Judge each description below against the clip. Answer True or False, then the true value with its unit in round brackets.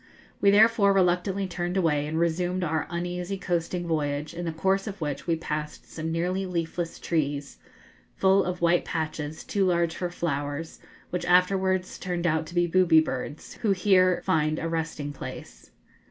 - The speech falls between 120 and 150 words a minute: False (165 wpm)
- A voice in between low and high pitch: True (175 Hz)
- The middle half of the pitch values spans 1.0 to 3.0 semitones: True (2.6 semitones)